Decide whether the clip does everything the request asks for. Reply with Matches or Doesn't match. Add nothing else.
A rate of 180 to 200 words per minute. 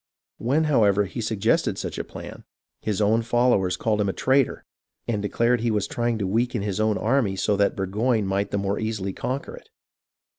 Matches